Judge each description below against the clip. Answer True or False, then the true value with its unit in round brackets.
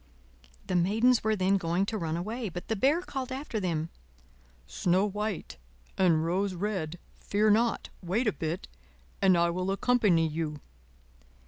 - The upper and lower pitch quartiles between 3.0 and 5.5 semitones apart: True (4.1 semitones)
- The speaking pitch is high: True (195 Hz)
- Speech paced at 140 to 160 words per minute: True (150 wpm)